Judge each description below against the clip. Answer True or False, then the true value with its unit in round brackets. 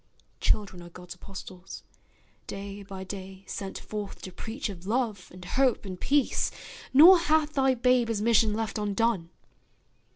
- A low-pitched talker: False (210 Hz)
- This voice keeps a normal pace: True (150 wpm)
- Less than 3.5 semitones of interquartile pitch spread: False (4.6 semitones)